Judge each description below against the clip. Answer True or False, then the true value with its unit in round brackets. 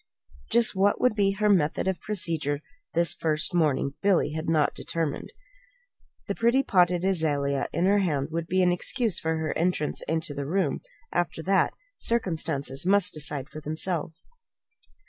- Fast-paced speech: False (150 wpm)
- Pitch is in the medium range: True (170 Hz)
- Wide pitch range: False (3.9 semitones)